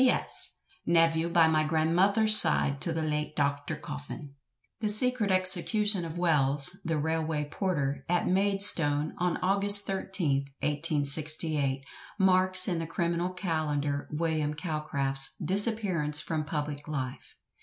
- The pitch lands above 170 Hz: No, medium, 160 Hz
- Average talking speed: No, slow, 125 wpm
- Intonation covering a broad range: No, average, 3.9 semitones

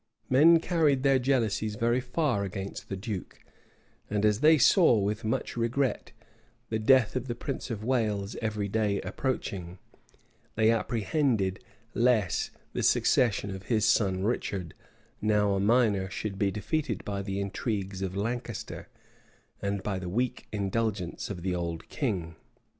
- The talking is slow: No, average, 145 wpm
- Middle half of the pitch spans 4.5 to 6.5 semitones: No, average, 3.7 semitones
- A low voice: Yes, low, 105 Hz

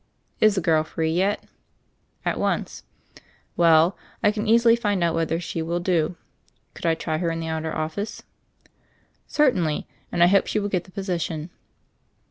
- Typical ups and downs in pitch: Yes, average, 3.7 semitones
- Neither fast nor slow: Yes, average, 175 wpm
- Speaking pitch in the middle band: Yes, medium, 175 Hz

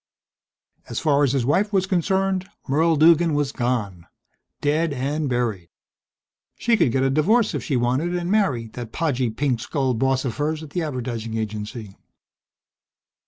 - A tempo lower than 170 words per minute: Yes, average, 160 wpm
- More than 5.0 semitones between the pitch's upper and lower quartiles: Yes, wide, 5.5 semitones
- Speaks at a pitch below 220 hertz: Yes, medium, 140 Hz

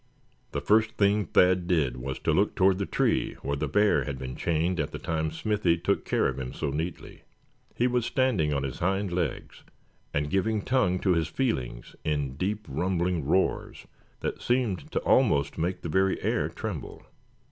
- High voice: No, very low, 90 Hz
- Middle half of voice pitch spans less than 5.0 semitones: No, average, 5.3 semitones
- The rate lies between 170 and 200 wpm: Yes, average, 180 wpm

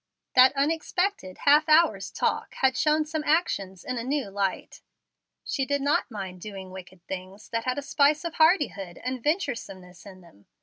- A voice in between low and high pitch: No, very high, 255 Hz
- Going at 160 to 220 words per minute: Yes, average, 170 wpm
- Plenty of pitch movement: Yes, wide, 7.9 semitones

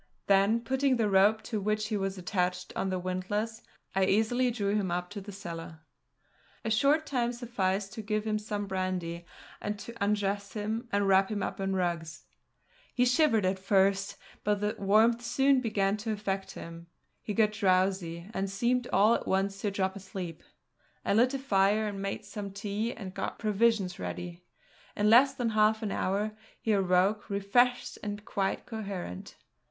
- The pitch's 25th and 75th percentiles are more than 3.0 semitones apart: No, narrow, 2.4 semitones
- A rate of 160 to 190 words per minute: Yes, average, 170 wpm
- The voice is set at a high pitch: Yes, high, 205 Hz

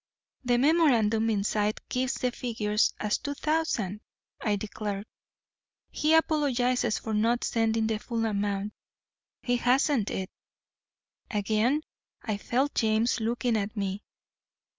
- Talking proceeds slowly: Yes, slow, 120 wpm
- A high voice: Yes, high, 225 Hz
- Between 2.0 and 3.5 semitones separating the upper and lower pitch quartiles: Yes, average, 3.1 semitones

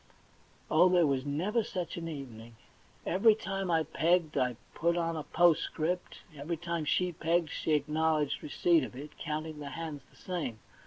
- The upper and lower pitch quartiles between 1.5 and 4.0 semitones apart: Yes, average, 2.9 semitones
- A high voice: No, medium, 160 Hz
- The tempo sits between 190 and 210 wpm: No, average, 165 wpm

